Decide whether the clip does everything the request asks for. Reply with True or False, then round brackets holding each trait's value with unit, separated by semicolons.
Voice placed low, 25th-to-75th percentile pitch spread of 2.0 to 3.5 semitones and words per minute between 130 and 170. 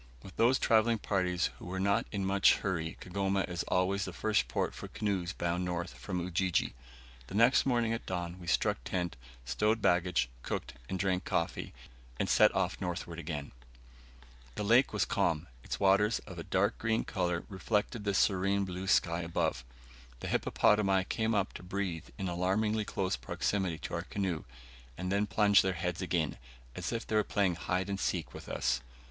False (95 Hz; 2.7 semitones; 180 wpm)